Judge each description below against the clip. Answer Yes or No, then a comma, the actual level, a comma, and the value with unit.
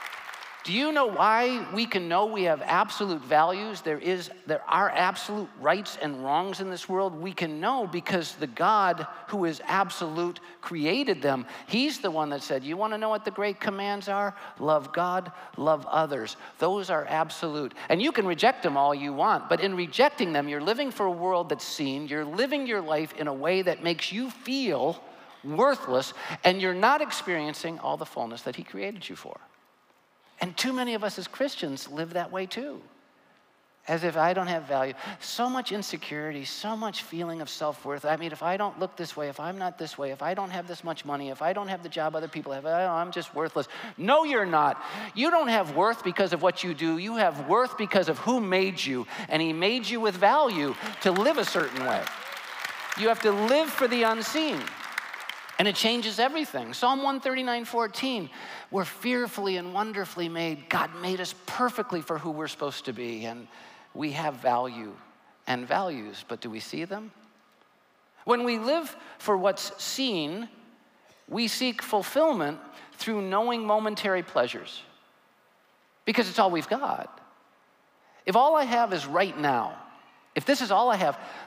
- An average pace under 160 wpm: No, average, 190 wpm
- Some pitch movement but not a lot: No, wide, 5.9 semitones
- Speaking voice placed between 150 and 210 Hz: Yes, medium, 185 Hz